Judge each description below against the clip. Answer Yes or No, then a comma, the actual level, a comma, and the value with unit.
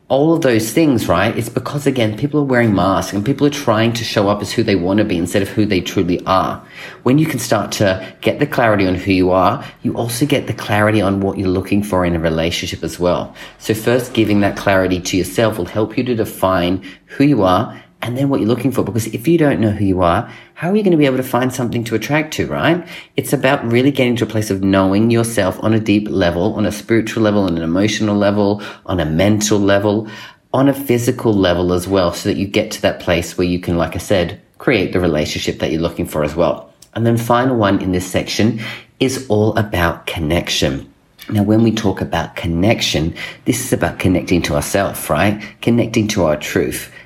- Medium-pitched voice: No, low, 105 Hz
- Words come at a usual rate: No, fast, 235 wpm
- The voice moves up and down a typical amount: Yes, average, 4.0 semitones